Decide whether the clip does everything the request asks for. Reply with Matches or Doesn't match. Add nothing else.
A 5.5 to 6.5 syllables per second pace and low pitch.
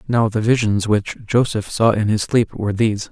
Doesn't match